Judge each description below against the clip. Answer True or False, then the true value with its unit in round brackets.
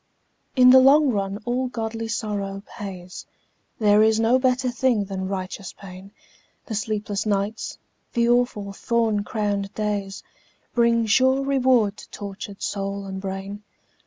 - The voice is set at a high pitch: True (210 Hz)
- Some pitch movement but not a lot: True (3.3 semitones)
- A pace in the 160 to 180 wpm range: False (135 wpm)